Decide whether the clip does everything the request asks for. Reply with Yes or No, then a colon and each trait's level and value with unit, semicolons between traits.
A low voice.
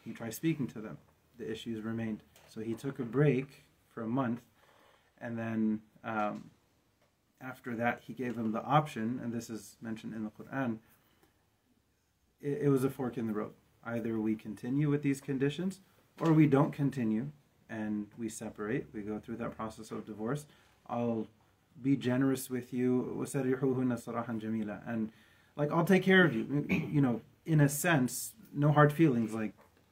Yes: low, 120 Hz